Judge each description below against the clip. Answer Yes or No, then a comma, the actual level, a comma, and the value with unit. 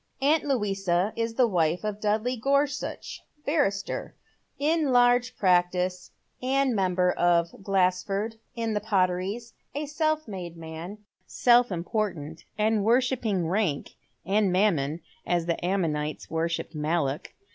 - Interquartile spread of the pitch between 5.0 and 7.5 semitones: Yes, wide, 5.4 semitones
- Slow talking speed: Yes, slow, 125 wpm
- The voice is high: Yes, high, 195 Hz